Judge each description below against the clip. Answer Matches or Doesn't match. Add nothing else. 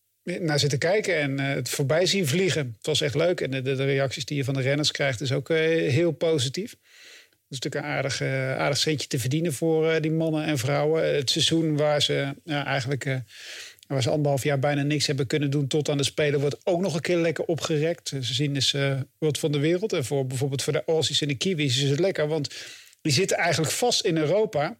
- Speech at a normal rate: Doesn't match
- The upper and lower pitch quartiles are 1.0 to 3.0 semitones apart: Matches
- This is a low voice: Doesn't match